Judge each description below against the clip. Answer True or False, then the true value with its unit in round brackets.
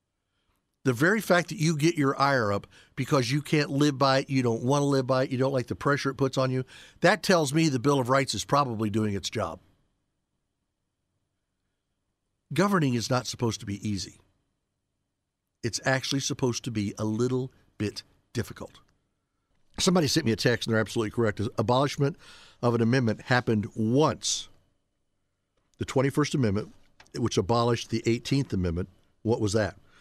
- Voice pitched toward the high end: False (115 Hz)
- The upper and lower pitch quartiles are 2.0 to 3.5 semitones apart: False (5.5 semitones)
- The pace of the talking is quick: False (170 wpm)